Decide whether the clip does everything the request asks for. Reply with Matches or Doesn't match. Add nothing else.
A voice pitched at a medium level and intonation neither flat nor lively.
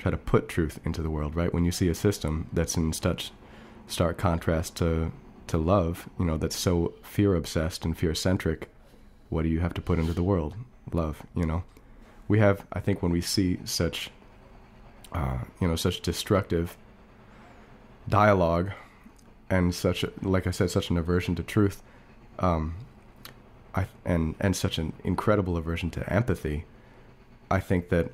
Doesn't match